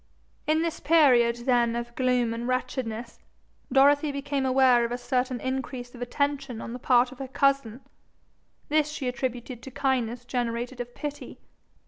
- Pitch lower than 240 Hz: No, very high, 255 Hz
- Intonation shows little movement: Yes, narrow, 2.3 semitones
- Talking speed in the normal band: Yes, average, 155 wpm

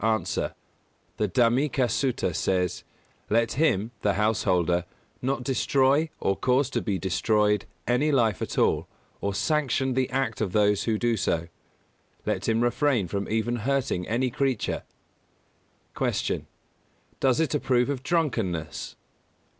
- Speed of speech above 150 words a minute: No, average, 140 wpm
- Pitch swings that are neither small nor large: Yes, average, 4.6 semitones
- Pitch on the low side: Yes, low, 115 Hz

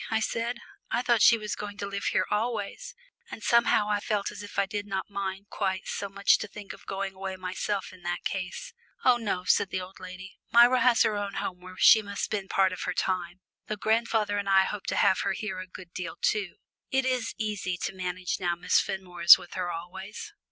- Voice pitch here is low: No, high, 200 Hz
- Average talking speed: No, fast, 225 wpm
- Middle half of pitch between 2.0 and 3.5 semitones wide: Yes, narrow, 2.4 semitones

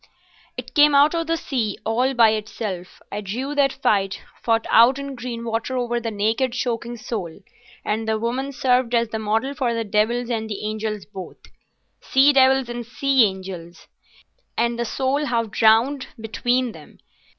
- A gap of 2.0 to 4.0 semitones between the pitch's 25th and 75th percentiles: Yes, average, 3.2 semitones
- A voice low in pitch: No, high, 235 Hz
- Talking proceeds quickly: No, average, 160 wpm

